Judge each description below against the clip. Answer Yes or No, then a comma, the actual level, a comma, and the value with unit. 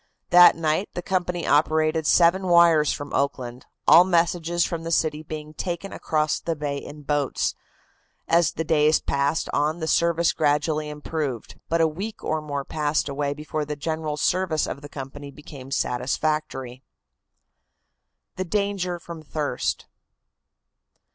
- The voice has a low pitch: No, medium, 155 Hz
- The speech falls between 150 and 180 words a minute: No, average, 140 wpm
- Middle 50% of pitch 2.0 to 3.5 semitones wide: Yes, narrow, 2.5 semitones